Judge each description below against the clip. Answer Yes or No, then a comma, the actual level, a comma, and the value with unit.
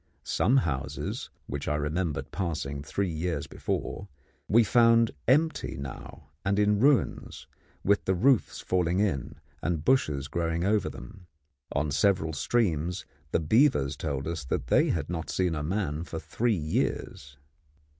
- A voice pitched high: No, very low, 85 Hz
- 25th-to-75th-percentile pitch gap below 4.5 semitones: No, wide, 5.6 semitones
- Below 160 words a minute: Yes, average, 145 wpm